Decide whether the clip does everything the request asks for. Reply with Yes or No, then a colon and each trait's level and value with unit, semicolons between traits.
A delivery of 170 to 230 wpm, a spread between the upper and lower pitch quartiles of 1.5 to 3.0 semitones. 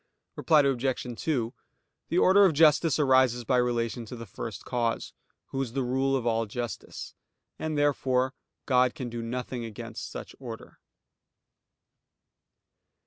No: average, 140 wpm; narrow, 2.5 semitones